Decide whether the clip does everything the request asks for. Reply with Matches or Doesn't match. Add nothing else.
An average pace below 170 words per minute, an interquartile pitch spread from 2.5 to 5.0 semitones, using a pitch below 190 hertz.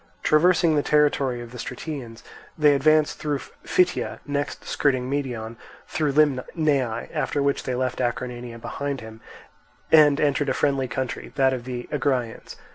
Matches